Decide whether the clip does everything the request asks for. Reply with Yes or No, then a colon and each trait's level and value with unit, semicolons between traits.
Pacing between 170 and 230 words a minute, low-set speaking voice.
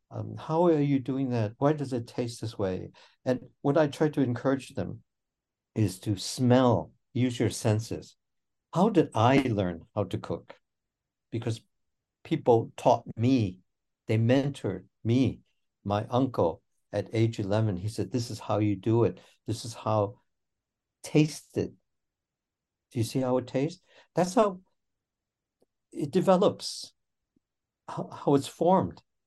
No: average, 145 wpm; low, 120 Hz